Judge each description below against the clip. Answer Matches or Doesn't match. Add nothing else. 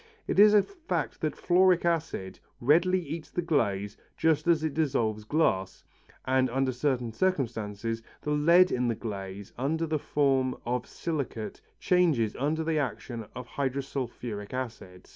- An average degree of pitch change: Doesn't match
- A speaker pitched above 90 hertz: Matches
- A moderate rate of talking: Matches